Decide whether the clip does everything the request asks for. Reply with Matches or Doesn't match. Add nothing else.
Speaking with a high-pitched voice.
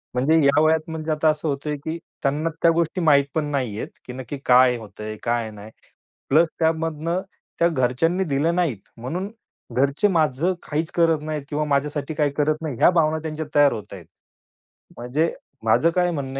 Doesn't match